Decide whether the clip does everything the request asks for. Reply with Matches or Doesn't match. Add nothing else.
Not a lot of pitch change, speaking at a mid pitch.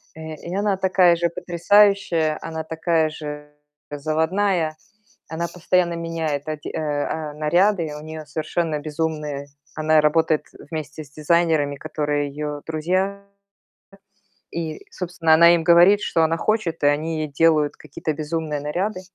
Matches